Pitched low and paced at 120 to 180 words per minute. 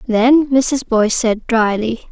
No: high, 240 Hz; average, 140 wpm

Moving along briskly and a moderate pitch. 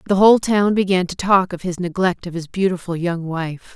Yes: fast, 225 wpm; medium, 180 Hz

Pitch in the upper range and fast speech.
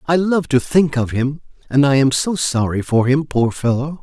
No: medium, 140 Hz; fast, 225 wpm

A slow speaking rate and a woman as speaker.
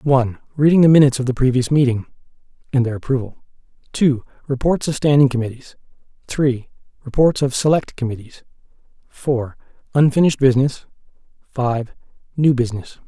No: slow, 125 wpm; male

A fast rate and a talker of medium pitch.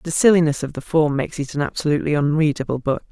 Yes: fast, 210 wpm; medium, 150 Hz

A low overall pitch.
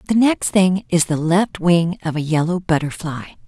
No: medium, 175 Hz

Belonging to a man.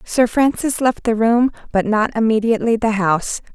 No: female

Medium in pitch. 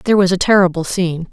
Yes: medium, 180 Hz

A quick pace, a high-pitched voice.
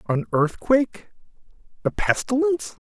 No: slow, 85 wpm; high, 200 Hz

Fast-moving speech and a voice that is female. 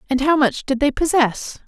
Yes: fast, 215 wpm; female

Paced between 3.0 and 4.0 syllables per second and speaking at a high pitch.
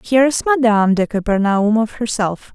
No: 5.3 syllables/s; high, 220 Hz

